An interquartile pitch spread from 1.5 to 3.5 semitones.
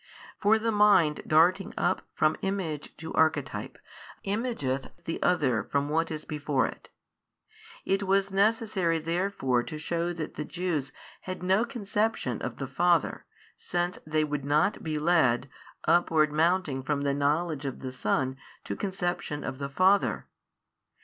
No: average, 4.7 semitones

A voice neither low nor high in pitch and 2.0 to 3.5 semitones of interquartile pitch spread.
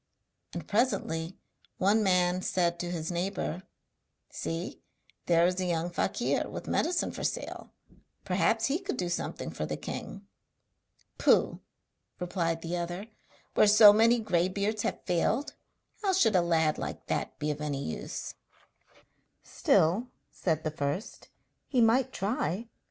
No: medium, 180 Hz; average, 4.3 semitones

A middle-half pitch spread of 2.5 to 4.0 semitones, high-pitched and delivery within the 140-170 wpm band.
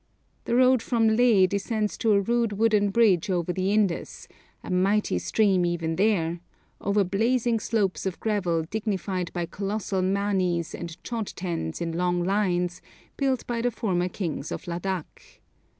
Yes: average, 3.6 semitones; high, 195 Hz; average, 150 wpm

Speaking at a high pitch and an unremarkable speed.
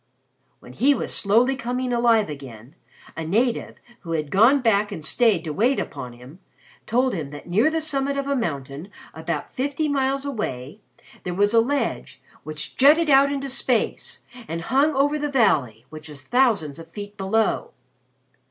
Yes: high, 225 Hz; average, 170 wpm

